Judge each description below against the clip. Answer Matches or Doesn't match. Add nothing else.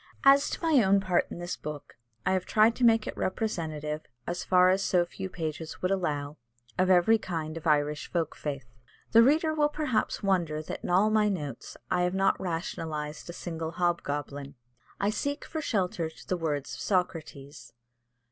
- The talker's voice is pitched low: Doesn't match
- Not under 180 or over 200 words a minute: Matches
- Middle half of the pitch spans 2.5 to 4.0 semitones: Doesn't match